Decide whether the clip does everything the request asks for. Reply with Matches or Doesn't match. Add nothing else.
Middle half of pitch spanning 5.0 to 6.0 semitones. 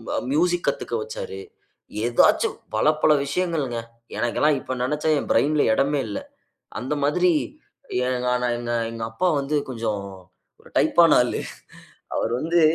Matches